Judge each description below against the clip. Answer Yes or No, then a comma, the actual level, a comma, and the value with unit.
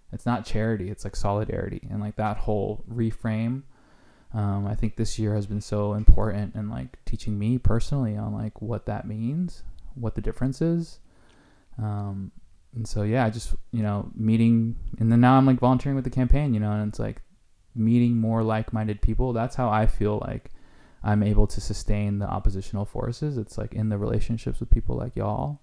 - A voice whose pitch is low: Yes, low, 110 Hz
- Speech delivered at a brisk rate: No, average, 190 wpm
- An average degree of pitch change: No, narrow, 2.3 semitones